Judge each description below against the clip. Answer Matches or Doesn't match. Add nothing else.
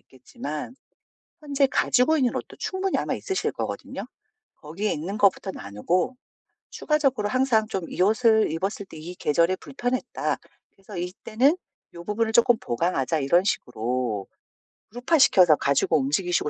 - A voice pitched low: Doesn't match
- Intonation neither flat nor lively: Doesn't match